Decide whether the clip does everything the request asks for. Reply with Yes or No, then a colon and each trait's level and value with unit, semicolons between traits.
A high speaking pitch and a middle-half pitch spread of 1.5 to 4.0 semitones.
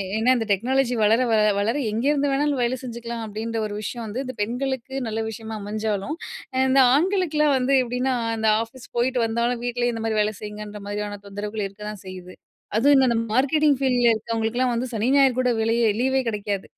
Yes: high, 235 Hz; average, 3.4 semitones